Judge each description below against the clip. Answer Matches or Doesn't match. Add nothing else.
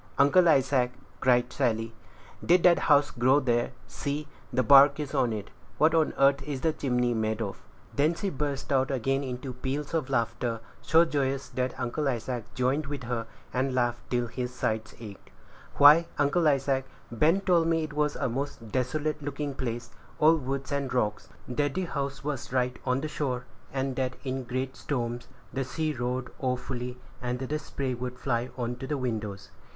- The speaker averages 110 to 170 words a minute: Doesn't match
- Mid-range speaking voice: Doesn't match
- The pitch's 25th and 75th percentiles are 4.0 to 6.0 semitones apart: Doesn't match